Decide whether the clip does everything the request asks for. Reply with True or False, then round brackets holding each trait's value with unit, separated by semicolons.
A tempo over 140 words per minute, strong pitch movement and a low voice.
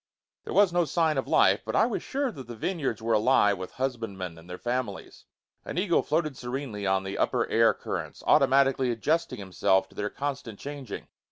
True (195 wpm; 6.2 semitones; 125 Hz)